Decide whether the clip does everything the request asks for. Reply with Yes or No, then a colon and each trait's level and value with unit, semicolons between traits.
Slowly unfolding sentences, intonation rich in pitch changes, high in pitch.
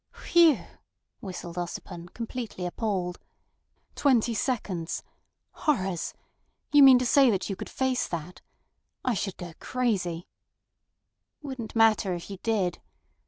Yes: slow, 120 wpm; wide, 6.0 semitones; high, 210 Hz